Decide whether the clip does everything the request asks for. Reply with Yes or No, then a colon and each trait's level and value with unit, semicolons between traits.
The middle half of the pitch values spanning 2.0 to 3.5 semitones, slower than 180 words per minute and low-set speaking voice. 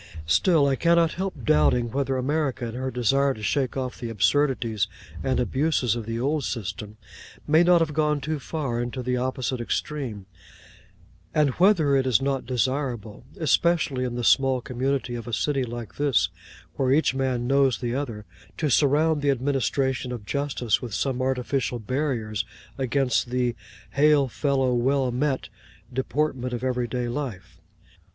Yes: average, 2.9 semitones; average, 155 wpm; low, 130 Hz